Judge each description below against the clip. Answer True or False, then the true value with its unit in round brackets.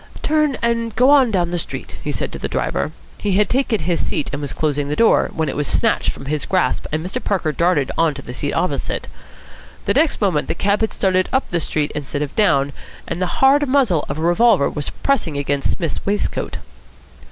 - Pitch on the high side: False (175 Hz)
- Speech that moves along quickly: True (220 wpm)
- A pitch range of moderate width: False (7.1 semitones)